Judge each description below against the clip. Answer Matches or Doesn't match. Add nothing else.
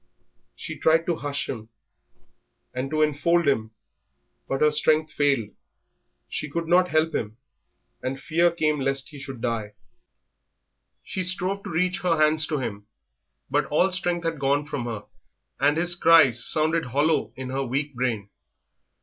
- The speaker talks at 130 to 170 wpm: Matches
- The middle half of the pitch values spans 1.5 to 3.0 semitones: Doesn't match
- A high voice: Doesn't match